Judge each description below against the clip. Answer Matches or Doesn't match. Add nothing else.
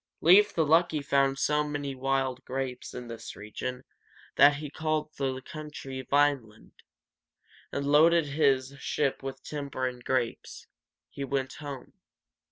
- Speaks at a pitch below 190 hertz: Matches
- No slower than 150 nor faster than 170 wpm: Doesn't match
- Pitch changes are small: Matches